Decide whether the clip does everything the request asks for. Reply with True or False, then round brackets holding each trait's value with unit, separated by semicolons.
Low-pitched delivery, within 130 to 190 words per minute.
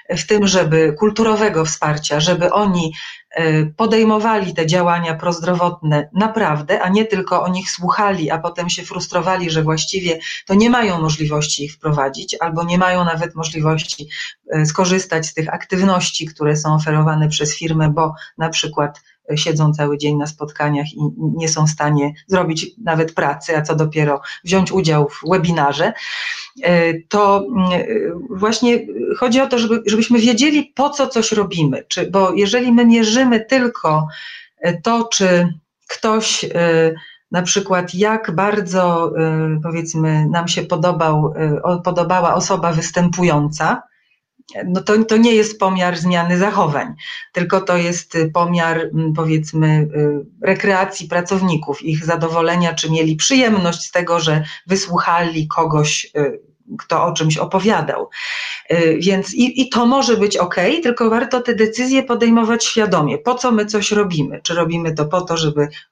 False (175 Hz; 135 wpm)